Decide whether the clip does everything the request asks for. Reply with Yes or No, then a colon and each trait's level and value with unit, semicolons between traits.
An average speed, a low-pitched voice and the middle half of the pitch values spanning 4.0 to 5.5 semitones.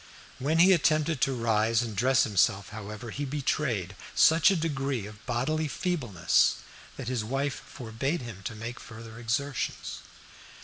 Yes: average, 145 wpm; low, 125 Hz; average, 4.6 semitones